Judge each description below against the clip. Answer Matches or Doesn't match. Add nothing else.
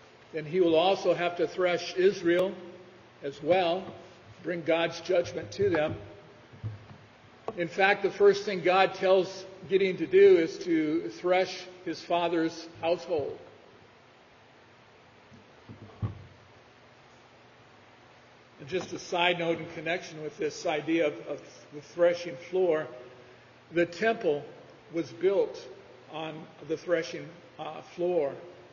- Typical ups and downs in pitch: Matches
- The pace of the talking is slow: Matches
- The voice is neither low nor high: Matches